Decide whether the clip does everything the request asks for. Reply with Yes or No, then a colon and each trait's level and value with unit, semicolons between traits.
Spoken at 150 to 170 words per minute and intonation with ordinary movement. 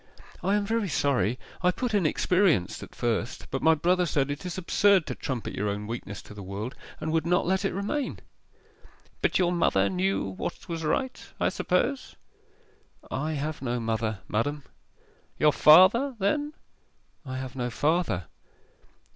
No: average, 160 wpm; wide, 8.0 semitones